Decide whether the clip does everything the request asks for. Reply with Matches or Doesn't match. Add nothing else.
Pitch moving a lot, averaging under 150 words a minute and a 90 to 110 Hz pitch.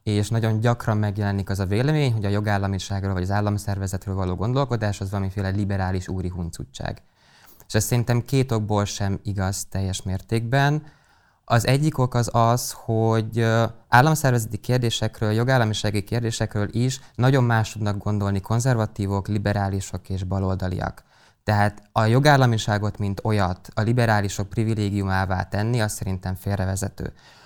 Doesn't match